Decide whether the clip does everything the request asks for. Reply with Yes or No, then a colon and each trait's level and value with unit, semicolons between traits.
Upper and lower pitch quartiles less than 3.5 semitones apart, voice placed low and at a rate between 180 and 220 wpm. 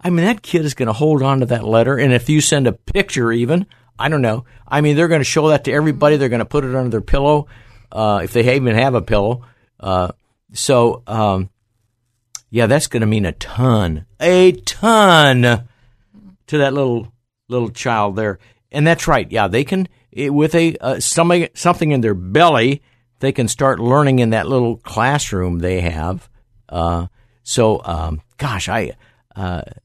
No: average, 4.9 semitones; low, 120 Hz; average, 190 wpm